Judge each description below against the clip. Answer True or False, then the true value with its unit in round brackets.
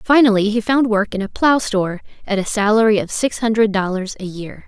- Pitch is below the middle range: False (210 Hz)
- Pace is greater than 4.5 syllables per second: True (5.6 syllables/s)